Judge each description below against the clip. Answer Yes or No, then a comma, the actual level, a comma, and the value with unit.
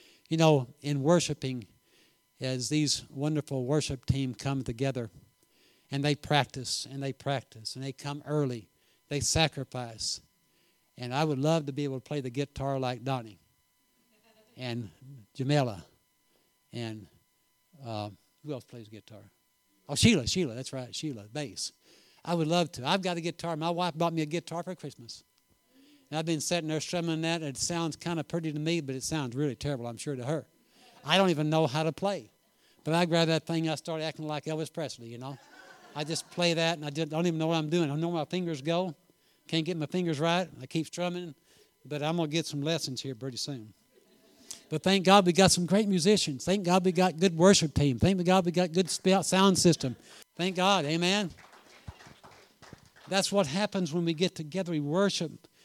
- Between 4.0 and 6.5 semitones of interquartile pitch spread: Yes, average, 4.3 semitones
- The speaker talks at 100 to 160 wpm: No, average, 195 wpm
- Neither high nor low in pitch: Yes, medium, 155 Hz